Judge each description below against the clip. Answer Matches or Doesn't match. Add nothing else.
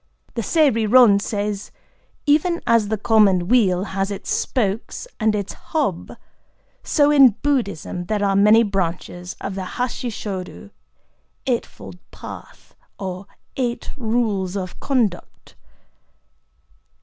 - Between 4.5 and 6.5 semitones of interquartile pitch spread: Doesn't match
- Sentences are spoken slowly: Matches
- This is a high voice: Matches